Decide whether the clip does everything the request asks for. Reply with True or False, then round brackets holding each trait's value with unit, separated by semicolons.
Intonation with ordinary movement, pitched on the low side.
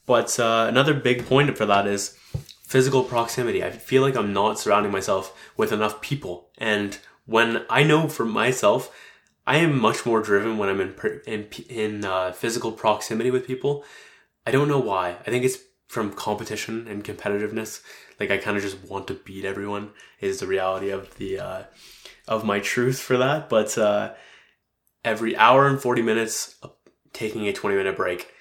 True (3.9 semitones; 110 Hz)